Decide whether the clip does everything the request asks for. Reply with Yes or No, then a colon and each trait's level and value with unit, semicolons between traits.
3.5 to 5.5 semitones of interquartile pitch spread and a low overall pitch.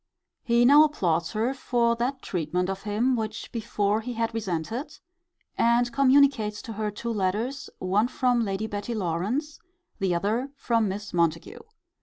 No: average, 3.8 semitones; high, 220 Hz